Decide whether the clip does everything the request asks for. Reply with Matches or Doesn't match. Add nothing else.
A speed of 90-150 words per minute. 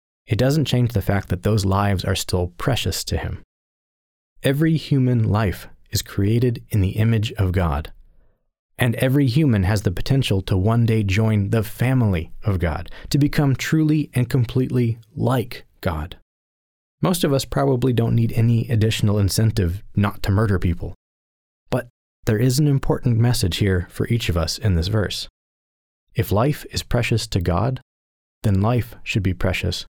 Doesn't match